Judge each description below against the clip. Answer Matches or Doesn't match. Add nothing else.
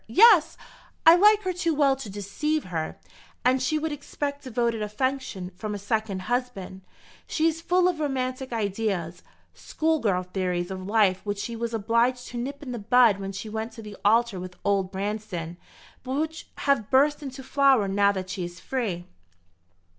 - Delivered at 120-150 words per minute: Doesn't match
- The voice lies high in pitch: Matches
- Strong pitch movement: Matches